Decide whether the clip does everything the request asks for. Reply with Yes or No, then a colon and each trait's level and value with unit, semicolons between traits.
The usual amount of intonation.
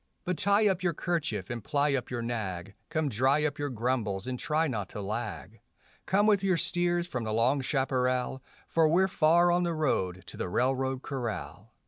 No: wide, 6.4 semitones